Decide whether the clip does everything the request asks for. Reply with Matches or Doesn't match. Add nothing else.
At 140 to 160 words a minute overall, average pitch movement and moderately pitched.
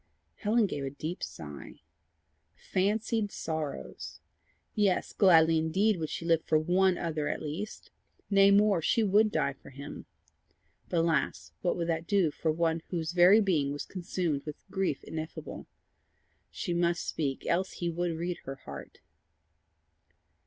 Matches